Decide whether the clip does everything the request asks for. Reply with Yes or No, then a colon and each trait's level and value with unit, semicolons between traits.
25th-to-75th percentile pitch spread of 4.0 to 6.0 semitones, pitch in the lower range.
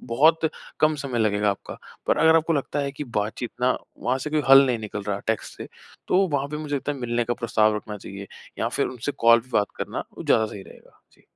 Yes: average, 5.1 semitones; low, 120 Hz